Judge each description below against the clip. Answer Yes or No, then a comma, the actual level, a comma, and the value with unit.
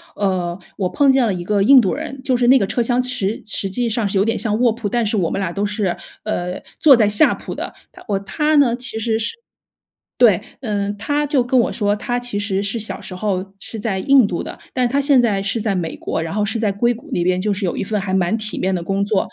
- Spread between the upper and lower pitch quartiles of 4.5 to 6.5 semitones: No, average, 3.8 semitones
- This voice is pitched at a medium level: No, high, 210 Hz